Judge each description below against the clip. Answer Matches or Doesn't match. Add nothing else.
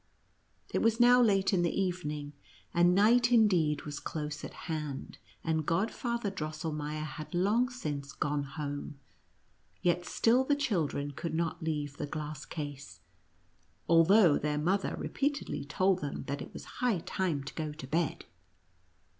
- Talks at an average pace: Matches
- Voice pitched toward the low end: Doesn't match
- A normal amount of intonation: Matches